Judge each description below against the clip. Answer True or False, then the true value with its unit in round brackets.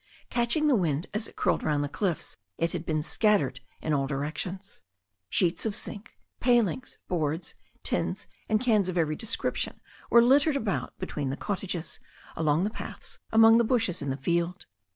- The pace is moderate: True (170 wpm)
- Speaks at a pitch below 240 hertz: True (185 Hz)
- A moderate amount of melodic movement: False (6.3 semitones)